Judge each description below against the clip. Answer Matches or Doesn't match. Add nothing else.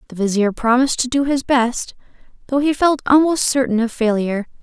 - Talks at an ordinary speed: Matches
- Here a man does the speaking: Doesn't match